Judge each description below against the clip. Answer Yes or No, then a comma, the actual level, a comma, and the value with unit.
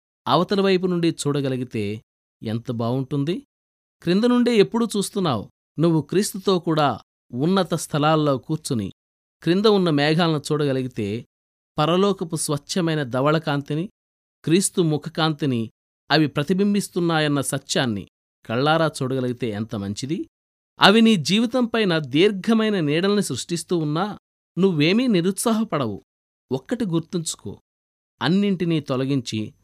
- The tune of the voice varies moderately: No, wide, 6.6 semitones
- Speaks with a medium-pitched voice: Yes, medium, 155 Hz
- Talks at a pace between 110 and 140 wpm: No, average, 90 wpm